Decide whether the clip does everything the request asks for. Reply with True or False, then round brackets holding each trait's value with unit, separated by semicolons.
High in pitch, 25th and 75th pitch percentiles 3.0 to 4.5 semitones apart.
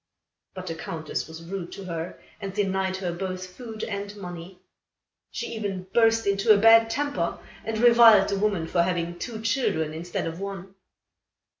True (195 Hz; 3.9 semitones)